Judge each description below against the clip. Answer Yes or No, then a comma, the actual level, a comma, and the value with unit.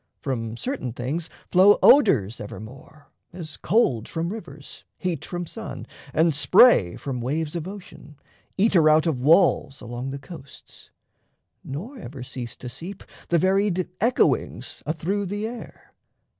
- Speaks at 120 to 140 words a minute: Yes, slow, 135 wpm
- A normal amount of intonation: No, wide, 6.2 semitones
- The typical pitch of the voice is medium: Yes, medium, 160 Hz